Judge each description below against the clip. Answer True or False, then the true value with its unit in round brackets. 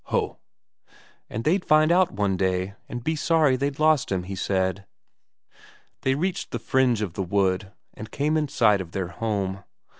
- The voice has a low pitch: True (110 Hz)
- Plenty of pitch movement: True (7.7 semitones)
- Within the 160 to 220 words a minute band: True (175 wpm)